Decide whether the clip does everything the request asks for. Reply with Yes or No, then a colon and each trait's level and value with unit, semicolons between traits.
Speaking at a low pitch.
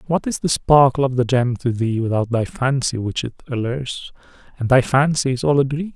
Yes: low, 130 Hz